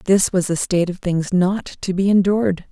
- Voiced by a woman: Yes, female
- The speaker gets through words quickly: Yes, fast, 220 wpm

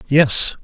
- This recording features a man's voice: Yes, male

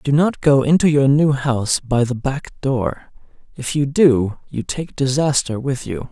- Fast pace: No, average, 185 wpm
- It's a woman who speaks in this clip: No, male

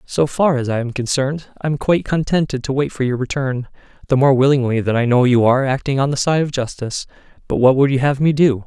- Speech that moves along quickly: Yes, fast, 240 wpm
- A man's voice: Yes, male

